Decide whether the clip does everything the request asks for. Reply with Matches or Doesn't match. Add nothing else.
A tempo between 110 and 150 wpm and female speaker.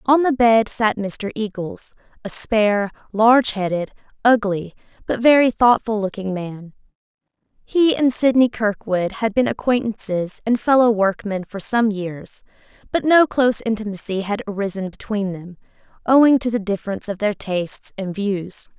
Matches